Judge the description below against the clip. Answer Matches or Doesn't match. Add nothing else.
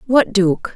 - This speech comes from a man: Doesn't match